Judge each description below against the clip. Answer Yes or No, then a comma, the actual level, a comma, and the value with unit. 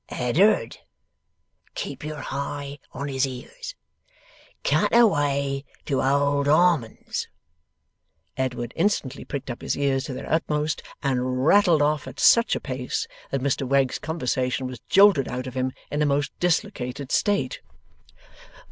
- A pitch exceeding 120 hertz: Yes, medium, 140 Hz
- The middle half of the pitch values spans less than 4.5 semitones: Yes, average, 2.9 semitones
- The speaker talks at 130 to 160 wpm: Yes, slow, 135 wpm